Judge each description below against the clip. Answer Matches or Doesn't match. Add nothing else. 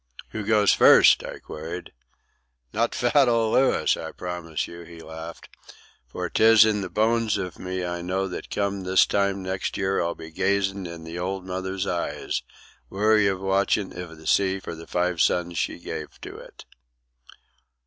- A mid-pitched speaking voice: Doesn't match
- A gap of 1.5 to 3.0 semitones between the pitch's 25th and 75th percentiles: Matches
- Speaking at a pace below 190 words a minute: Matches